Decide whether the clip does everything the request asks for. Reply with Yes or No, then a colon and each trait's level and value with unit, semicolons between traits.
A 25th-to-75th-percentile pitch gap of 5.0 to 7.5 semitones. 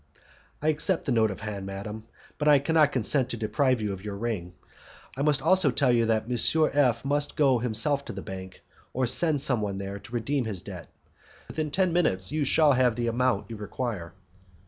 Yes: average, 5.3 semitones